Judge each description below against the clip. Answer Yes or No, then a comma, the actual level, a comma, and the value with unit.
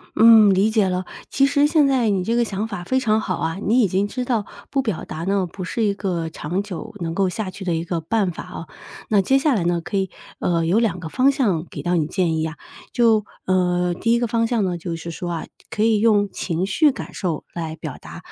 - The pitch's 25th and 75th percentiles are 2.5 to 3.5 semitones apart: No, average, 4.6 semitones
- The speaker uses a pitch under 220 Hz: Yes, high, 195 Hz